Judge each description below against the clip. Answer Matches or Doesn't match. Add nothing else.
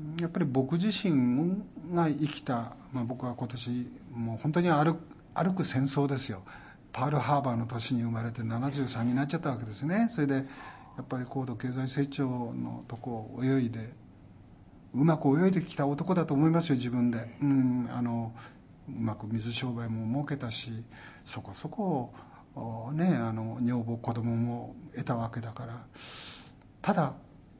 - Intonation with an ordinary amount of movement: Matches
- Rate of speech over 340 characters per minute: Doesn't match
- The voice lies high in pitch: Doesn't match